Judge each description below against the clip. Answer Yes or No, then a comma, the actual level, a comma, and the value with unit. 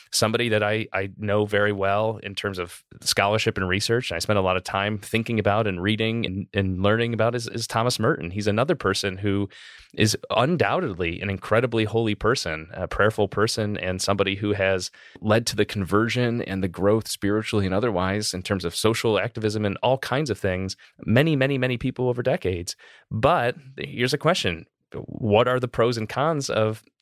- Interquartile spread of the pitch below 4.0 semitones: Yes, average, 2.7 semitones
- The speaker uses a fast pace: No, average, 190 wpm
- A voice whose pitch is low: Yes, low, 105 Hz